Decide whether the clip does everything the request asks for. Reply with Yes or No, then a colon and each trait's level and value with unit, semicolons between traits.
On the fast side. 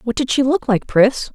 Yes: fast, 270 wpm